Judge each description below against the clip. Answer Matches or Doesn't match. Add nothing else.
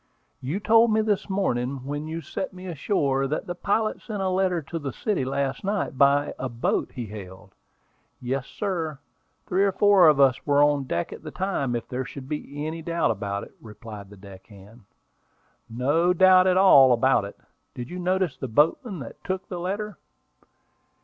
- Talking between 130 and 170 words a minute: Doesn't match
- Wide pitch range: Matches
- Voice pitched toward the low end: Doesn't match